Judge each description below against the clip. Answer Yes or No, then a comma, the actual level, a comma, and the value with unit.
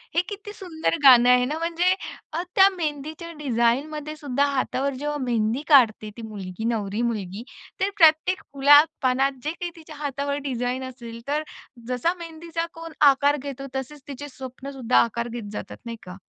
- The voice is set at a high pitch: Yes, very high, 280 Hz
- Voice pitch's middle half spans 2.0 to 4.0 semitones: No, average, 4.5 semitones